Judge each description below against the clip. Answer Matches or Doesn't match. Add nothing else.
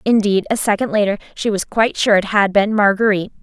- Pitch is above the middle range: Matches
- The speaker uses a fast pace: Matches